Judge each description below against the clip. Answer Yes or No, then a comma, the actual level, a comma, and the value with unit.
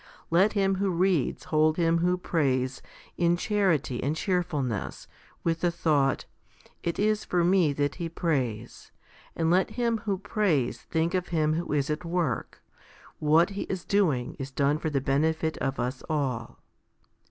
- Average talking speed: Yes, average, 170 wpm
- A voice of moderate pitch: Yes, medium, 165 Hz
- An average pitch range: Yes, average, 4.2 semitones